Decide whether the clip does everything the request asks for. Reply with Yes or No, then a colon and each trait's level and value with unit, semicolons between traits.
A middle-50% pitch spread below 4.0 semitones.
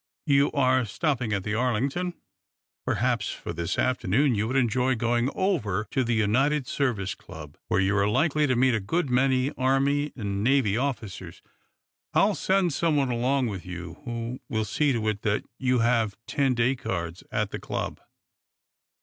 No: average, 4.4 semitones